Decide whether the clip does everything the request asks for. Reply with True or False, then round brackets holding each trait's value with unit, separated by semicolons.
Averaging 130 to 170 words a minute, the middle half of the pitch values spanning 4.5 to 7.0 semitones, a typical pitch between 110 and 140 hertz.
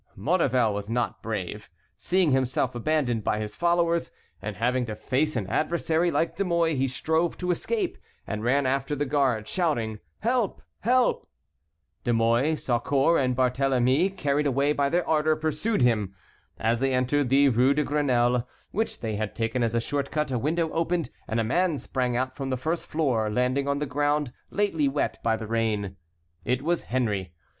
False (180 wpm; 5.0 semitones; 135 Hz)